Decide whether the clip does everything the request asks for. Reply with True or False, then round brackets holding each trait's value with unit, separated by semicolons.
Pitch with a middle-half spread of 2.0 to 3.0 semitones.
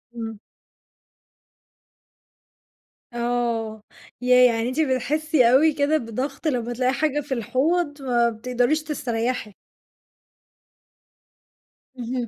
False (3.5 semitones)